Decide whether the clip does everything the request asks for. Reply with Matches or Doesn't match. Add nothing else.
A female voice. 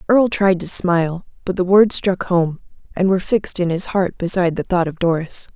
Matches